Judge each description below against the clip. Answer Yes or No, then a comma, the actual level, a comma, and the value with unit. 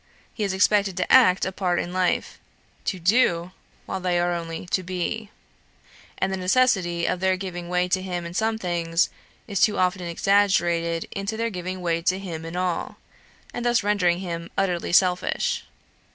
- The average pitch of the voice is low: No, medium, 185 Hz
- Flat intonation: Yes, narrow, 2.1 semitones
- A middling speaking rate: Yes, average, 175 wpm